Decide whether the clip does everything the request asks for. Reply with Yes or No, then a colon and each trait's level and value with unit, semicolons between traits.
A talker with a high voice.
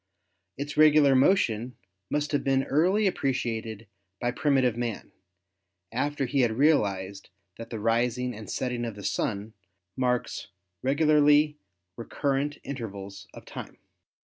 No: low, 125 Hz